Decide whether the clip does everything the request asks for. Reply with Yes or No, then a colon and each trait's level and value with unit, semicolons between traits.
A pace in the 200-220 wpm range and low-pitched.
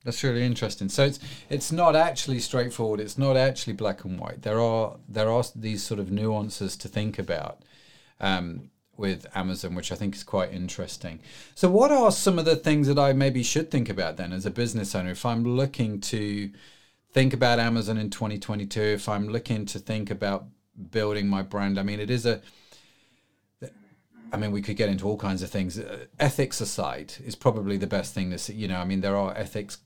Yes: fast, 205 wpm; low, 105 Hz